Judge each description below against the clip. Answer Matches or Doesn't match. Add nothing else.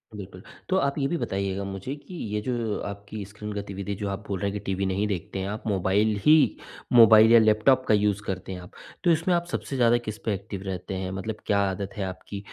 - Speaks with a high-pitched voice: Doesn't match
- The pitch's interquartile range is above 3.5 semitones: Doesn't match